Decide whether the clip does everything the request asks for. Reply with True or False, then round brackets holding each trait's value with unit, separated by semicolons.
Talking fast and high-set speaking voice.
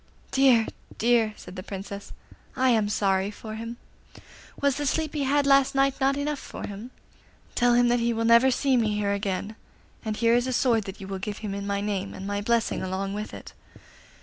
True (210 wpm; 225 Hz)